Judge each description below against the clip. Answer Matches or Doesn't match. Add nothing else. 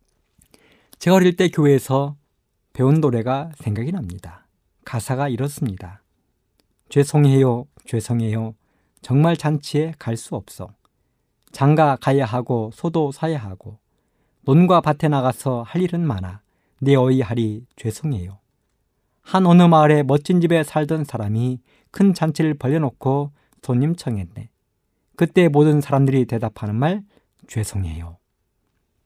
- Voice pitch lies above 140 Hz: Doesn't match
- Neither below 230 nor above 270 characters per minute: Matches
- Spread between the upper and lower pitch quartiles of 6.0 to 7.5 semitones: Doesn't match